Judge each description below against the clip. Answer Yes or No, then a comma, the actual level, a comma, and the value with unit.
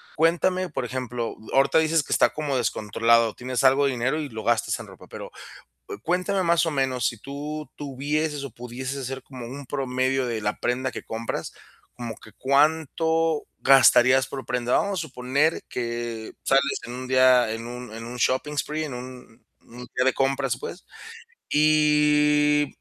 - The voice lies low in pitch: Yes, low, 130 Hz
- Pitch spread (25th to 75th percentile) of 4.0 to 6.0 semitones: No, average, 3.3 semitones